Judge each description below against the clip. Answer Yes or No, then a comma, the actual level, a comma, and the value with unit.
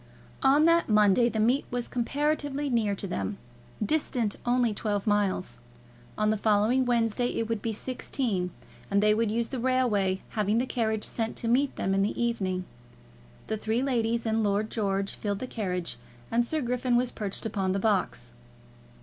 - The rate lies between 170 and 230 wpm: Yes, average, 175 wpm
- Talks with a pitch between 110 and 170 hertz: No, high, 225 Hz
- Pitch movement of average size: Yes, average, 3.3 semitones